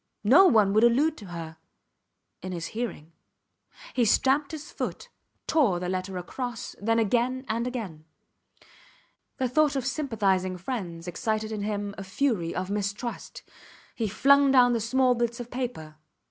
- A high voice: Yes, high, 225 Hz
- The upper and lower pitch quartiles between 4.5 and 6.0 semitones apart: Yes, average, 5.2 semitones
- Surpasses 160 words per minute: No, average, 150 wpm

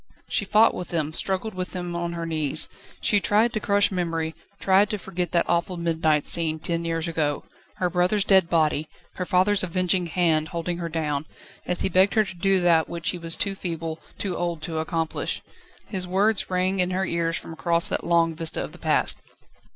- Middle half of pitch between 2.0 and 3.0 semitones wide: Yes, narrow, 2.4 semitones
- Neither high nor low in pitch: Yes, medium, 175 Hz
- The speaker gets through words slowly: No, average, 200 wpm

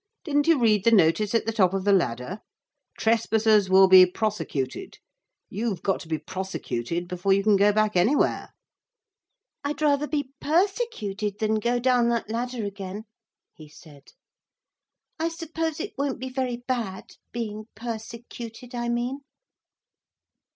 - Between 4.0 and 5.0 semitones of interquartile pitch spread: Yes, average, 4.5 semitones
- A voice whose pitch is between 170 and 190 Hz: No, high, 220 Hz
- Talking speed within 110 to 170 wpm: Yes, average, 145 wpm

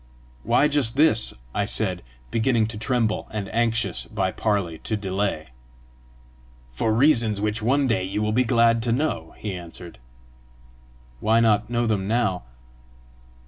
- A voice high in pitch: No, low, 110 Hz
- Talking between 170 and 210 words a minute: No, average, 145 wpm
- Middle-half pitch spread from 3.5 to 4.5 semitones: No, narrow, 2.6 semitones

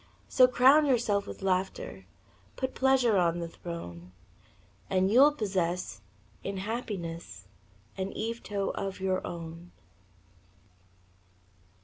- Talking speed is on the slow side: Yes, slow, 100 wpm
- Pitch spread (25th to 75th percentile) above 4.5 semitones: Yes, wide, 5.5 semitones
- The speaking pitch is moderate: No, high, 195 Hz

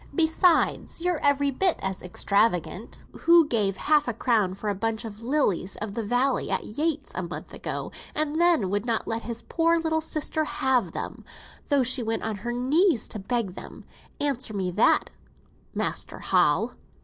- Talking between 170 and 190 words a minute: Yes, average, 175 wpm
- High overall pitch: Yes, high, 245 Hz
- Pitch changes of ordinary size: No, wide, 6.4 semitones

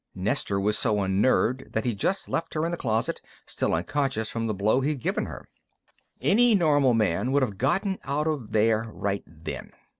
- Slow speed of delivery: No, average, 185 wpm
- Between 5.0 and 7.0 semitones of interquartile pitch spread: Yes, wide, 5.6 semitones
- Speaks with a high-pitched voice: No, low, 120 Hz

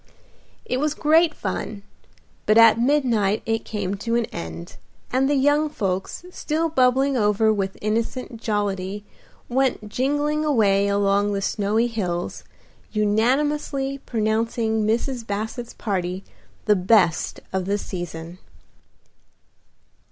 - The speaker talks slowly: Yes, slow, 115 wpm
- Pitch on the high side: Yes, high, 220 Hz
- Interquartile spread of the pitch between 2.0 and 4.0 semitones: No, average, 4.6 semitones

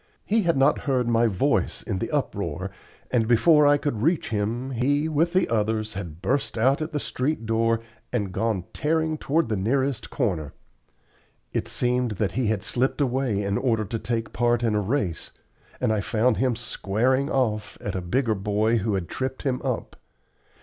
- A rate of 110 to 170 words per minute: No, average, 185 wpm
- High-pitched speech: No, low, 120 Hz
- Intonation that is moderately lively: Yes, average, 4.0 semitones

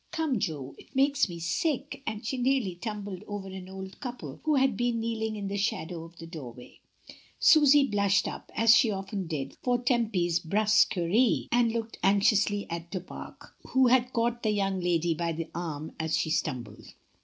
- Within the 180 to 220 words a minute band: Yes, average, 185 wpm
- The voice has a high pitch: Yes, high, 205 Hz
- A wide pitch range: Yes, wide, 5.7 semitones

